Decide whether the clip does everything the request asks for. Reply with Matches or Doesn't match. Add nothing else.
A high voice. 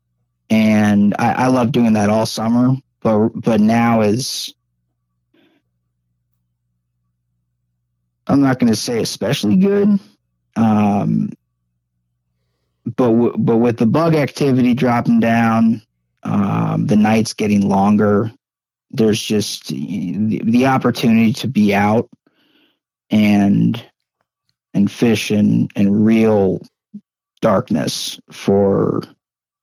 Doesn't match